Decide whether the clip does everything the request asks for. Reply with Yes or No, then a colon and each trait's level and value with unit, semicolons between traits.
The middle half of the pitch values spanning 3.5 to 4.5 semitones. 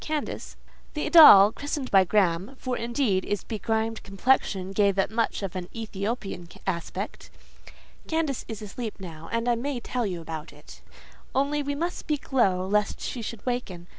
No: average, 4.9 semitones